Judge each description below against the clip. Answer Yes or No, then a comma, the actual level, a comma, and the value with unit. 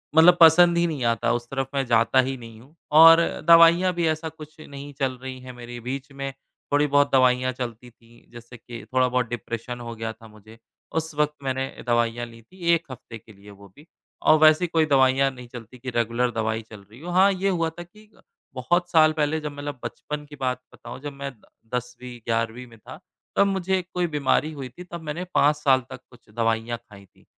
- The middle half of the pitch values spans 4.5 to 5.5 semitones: Yes, average, 4.8 semitones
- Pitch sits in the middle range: No, low, 130 Hz